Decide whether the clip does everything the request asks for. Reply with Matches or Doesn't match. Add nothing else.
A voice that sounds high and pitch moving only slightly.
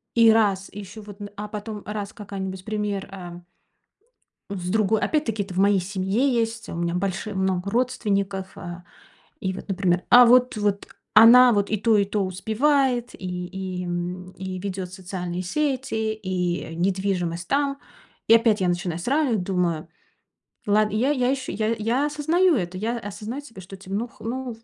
Doesn't match